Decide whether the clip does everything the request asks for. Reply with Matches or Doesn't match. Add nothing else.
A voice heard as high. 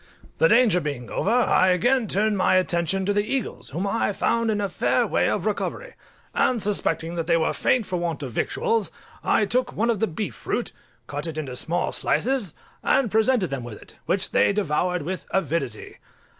Matches